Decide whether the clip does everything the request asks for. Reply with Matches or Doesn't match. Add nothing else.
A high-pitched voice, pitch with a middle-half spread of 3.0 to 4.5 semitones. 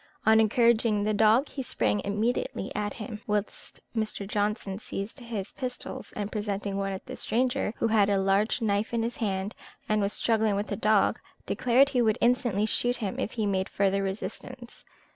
Doesn't match